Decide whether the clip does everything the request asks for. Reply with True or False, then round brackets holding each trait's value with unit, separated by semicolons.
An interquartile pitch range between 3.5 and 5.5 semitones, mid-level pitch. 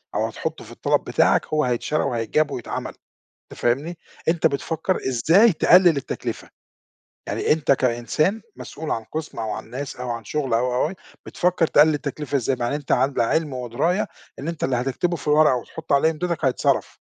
True (4.4 semitones; 145 Hz)